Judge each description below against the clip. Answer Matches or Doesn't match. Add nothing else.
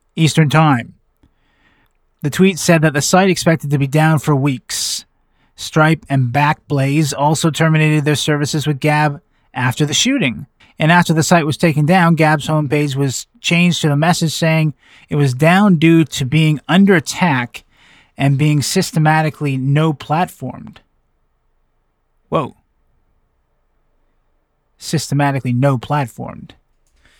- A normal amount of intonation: Doesn't match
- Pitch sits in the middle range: Matches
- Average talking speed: Doesn't match